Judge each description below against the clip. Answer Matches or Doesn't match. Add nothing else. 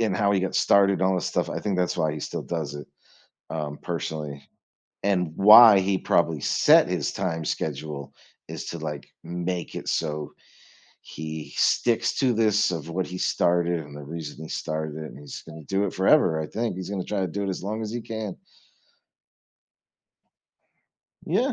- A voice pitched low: Matches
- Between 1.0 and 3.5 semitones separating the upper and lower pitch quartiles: Doesn't match